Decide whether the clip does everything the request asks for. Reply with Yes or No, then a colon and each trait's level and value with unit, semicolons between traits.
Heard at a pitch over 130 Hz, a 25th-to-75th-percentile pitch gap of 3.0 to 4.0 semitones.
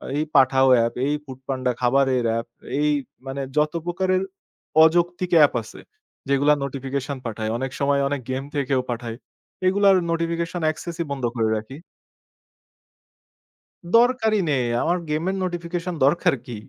No: medium, 140 Hz; average, 4.7 semitones